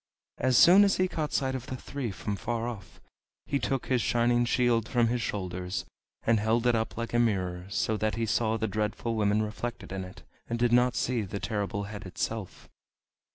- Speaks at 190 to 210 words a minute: Yes, average, 200 wpm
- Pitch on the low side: Yes, low, 115 Hz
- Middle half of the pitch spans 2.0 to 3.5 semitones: Yes, average, 2.8 semitones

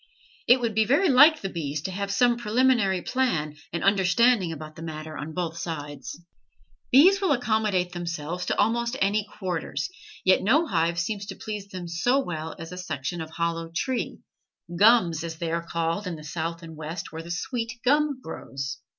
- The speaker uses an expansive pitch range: Yes, wide, 6.1 semitones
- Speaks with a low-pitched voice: No, medium, 180 Hz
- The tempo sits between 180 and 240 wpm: Yes, average, 185 wpm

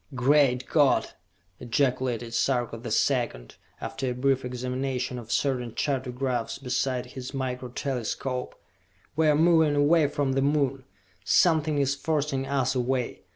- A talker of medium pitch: No, low, 130 Hz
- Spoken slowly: Yes, slow, 130 wpm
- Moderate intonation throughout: No, narrow, 2.1 semitones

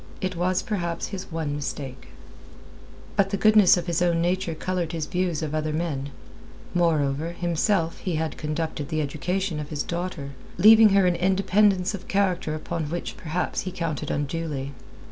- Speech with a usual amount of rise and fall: Yes, average, 3.1 semitones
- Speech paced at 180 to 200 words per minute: No, average, 165 wpm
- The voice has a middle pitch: Yes, medium, 170 Hz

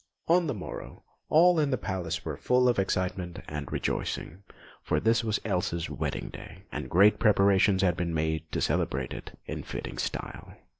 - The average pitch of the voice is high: No, very low, 95 Hz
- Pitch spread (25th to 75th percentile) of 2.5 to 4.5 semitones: No, average, 5.2 semitones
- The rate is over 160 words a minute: Yes, average, 170 wpm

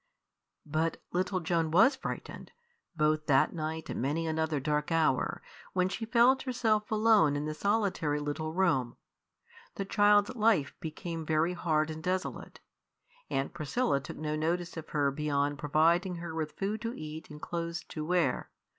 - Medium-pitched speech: Yes, medium, 160 Hz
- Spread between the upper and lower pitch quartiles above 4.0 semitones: No, average, 3.7 semitones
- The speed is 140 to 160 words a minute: Yes, average, 155 wpm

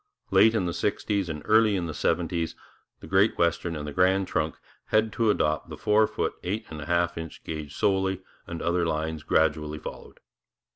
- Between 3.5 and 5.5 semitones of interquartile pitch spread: Yes, average, 3.9 semitones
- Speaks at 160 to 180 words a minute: No, average, 190 wpm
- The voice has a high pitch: No, very low, 85 Hz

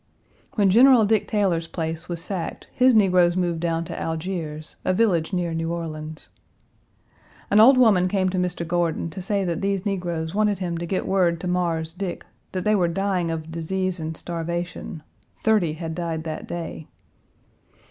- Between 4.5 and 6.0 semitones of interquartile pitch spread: No, average, 2.9 semitones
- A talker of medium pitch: Yes, medium, 175 Hz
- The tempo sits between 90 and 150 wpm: No, average, 170 wpm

